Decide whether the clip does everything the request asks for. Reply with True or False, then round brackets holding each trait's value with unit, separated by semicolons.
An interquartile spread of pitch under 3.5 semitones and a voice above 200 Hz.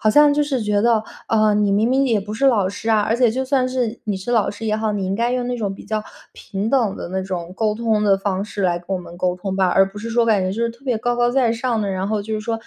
True (3.1 semitones; 215 Hz)